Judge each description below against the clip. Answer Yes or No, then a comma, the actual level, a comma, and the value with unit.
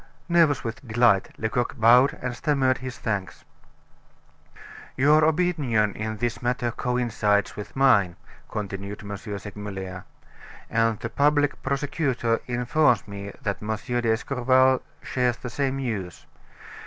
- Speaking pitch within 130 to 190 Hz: No, low, 120 Hz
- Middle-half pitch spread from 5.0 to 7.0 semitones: No, average, 4.1 semitones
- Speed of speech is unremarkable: No, slow, 115 wpm